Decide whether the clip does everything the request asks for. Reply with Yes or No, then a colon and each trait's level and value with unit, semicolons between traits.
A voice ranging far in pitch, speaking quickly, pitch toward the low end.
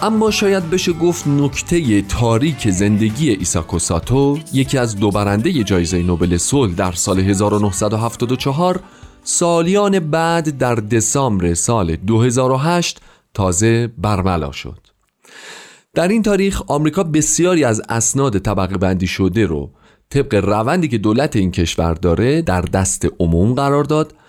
No: wide, 8.1 semitones; average, 125 wpm; low, 115 Hz